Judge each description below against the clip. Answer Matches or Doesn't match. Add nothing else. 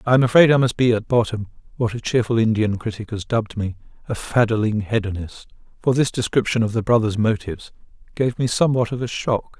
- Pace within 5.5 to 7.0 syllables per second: Matches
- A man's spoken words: Matches